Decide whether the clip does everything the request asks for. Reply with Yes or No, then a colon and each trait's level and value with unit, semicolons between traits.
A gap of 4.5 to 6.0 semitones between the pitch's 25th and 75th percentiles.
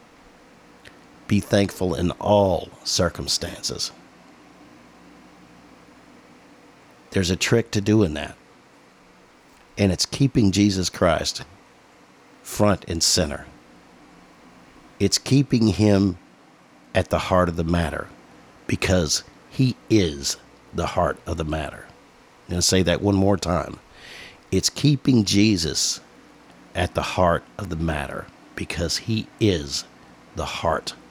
No: average, 3.8 semitones